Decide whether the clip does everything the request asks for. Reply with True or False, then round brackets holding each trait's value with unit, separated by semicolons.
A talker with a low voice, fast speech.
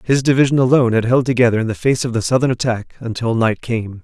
True (120 Hz; 240 wpm)